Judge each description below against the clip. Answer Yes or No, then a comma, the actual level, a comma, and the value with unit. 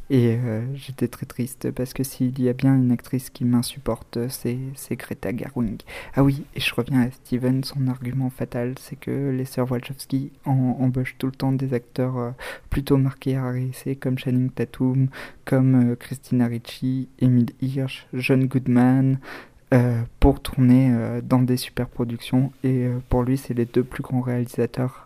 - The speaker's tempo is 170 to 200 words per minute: Yes, average, 175 wpm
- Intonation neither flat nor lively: No, narrow, 1.5 semitones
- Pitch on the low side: Yes, low, 130 Hz